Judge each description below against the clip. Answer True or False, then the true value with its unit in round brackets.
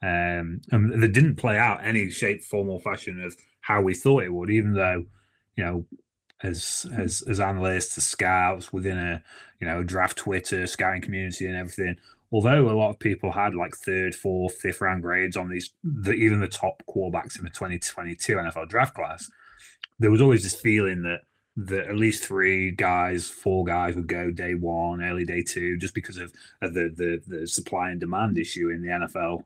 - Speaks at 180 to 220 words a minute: True (200 wpm)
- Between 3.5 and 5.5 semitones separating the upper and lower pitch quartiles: False (3.1 semitones)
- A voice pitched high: False (95 Hz)